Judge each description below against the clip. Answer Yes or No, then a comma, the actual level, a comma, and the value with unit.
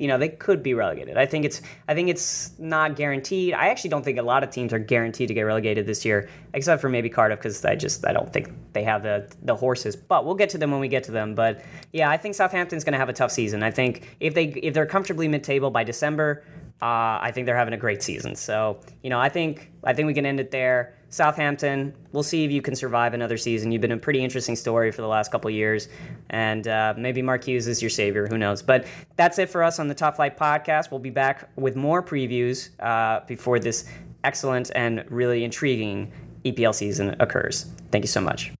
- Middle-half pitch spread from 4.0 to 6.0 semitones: Yes, average, 4.7 semitones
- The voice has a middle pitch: No, low, 130 Hz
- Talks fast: Yes, fast, 240 wpm